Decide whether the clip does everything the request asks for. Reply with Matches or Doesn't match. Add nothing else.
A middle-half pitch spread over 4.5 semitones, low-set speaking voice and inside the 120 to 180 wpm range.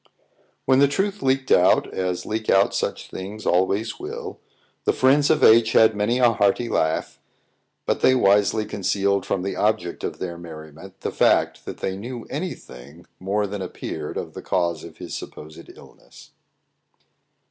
Matches